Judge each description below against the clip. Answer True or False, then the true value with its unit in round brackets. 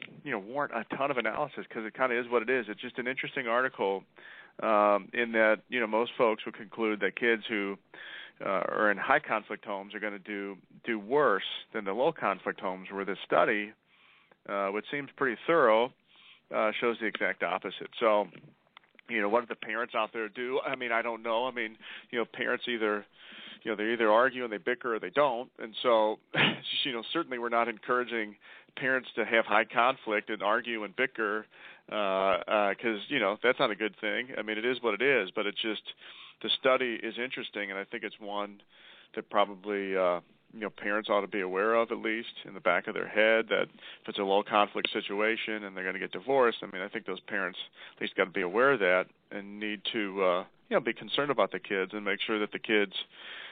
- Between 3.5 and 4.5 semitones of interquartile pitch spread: False (2.4 semitones)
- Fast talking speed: True (225 wpm)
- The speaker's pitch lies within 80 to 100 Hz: False (110 Hz)